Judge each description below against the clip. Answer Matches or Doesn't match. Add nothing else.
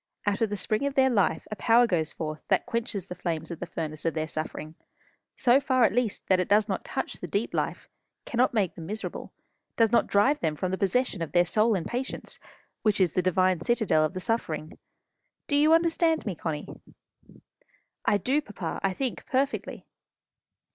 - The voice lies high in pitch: Matches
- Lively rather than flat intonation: Matches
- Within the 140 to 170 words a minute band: Doesn't match